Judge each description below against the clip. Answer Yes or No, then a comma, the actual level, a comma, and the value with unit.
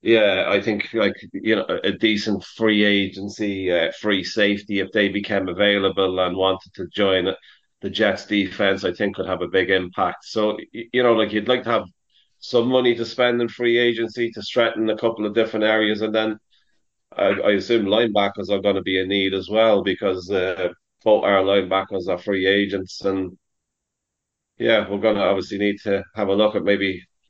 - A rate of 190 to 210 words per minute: Yes, average, 195 wpm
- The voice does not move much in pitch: Yes, narrow, 2.2 semitones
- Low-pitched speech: Yes, low, 100 Hz